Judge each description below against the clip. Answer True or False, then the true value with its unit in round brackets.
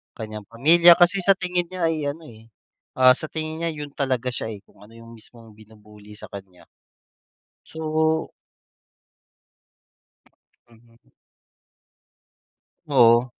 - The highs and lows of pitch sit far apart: True (6.3 semitones)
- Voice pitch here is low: True (125 Hz)